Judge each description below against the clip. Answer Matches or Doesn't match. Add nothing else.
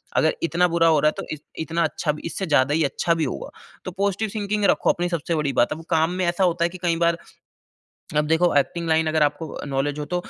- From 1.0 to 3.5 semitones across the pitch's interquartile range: Matches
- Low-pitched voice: Doesn't match